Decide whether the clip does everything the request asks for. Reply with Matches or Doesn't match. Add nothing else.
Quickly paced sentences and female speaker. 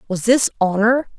Doesn't match